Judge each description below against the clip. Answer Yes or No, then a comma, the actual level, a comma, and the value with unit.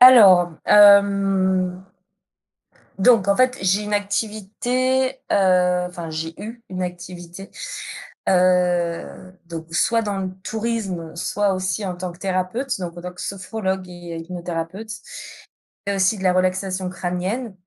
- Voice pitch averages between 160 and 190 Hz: Yes, medium, 185 Hz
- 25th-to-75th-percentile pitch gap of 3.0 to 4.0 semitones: No, narrow, 2.4 semitones